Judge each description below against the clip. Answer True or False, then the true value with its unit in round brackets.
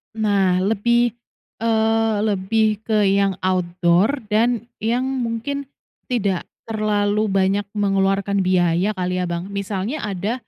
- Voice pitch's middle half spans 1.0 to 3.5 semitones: True (2.9 semitones)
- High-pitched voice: True (205 Hz)